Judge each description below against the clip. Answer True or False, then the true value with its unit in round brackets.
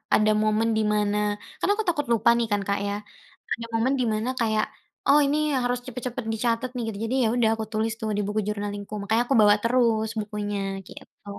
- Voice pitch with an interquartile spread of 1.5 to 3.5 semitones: True (2.7 semitones)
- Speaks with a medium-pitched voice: False (220 Hz)